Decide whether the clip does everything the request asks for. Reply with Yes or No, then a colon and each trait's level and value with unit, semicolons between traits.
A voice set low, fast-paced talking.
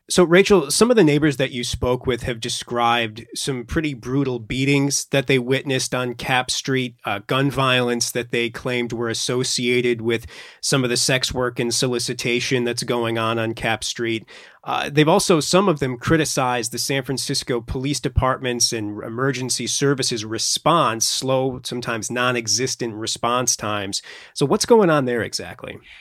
No: low, 125 Hz; average, 165 wpm